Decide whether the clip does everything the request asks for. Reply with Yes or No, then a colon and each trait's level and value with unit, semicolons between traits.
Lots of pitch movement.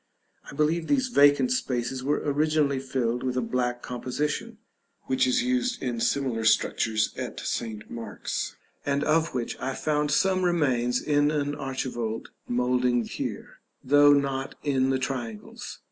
No: average, 3.5 semitones